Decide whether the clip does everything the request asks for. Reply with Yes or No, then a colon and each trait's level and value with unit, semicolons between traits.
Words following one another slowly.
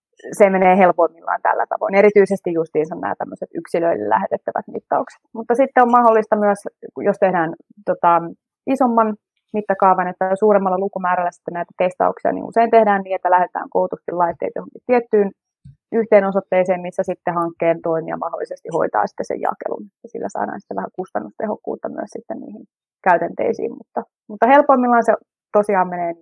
No: average, 145 wpm